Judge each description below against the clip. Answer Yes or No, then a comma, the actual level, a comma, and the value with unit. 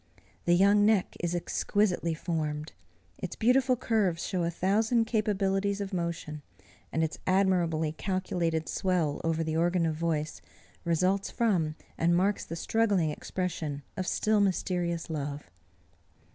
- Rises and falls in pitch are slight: No, average, 3.6 semitones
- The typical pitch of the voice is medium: Yes, medium, 175 Hz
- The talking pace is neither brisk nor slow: No, slow, 130 wpm